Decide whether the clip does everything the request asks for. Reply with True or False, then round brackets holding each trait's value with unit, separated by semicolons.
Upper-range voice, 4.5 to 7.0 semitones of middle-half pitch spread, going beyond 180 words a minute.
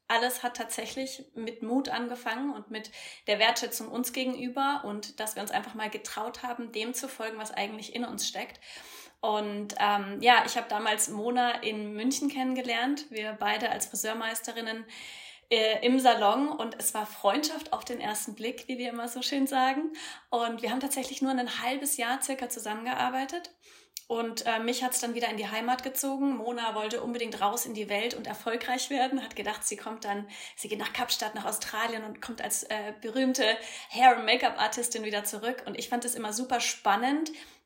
False (240 Hz; 3.0 semitones; 190 wpm)